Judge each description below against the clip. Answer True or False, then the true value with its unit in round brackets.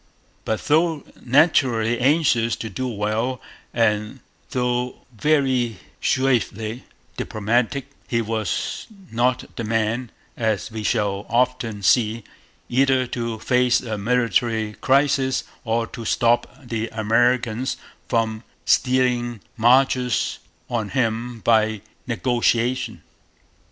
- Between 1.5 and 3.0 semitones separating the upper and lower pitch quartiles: True (2.4 semitones)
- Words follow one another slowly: True (100 wpm)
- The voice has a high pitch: False (120 Hz)